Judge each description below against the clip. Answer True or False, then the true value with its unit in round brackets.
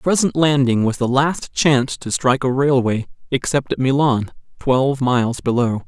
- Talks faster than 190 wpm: False (175 wpm)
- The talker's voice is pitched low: True (130 Hz)